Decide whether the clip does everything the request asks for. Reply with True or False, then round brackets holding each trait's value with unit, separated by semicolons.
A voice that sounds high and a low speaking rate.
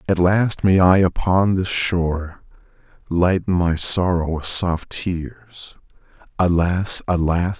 False (90 Hz; 120 wpm)